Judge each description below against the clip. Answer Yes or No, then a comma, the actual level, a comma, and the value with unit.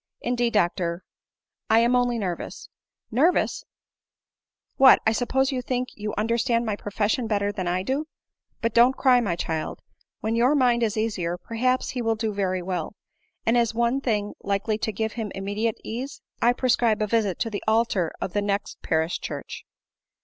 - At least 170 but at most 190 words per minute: Yes, average, 185 wpm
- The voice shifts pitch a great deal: No, average, 3.1 semitones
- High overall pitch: Yes, high, 220 Hz